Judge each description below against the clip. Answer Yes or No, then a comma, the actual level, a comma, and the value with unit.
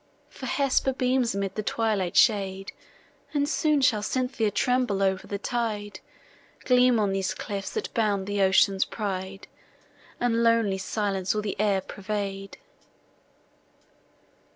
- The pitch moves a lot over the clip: No, average, 3.6 semitones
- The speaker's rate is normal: No, slow, 130 wpm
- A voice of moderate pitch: No, high, 210 Hz